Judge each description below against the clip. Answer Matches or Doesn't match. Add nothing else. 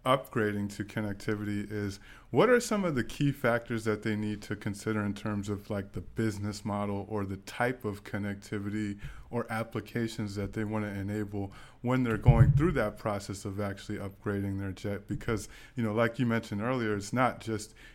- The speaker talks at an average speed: Matches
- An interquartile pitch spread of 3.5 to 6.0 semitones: Doesn't match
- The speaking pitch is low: Matches